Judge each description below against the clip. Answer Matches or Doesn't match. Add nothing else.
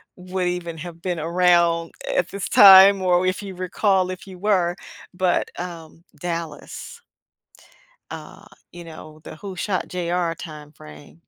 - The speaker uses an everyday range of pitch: Doesn't match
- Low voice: Doesn't match